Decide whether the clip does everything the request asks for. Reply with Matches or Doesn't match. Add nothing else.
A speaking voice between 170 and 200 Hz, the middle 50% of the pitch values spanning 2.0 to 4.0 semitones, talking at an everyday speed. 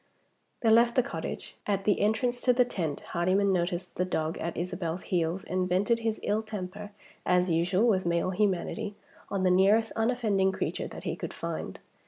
Matches